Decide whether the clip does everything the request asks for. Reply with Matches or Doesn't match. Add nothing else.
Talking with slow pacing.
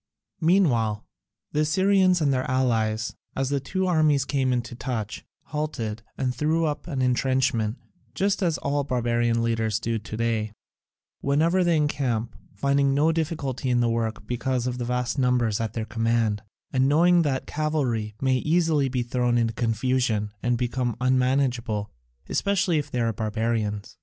Doesn't match